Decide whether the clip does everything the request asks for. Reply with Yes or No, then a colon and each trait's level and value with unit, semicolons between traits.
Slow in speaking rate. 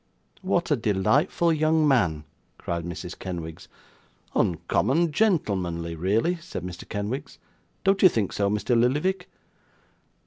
Yes: slow, 115 wpm